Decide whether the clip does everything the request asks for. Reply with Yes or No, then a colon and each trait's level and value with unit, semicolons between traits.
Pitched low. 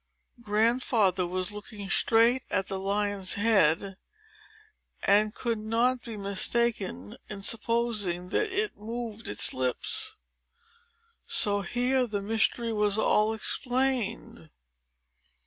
No: high, 215 Hz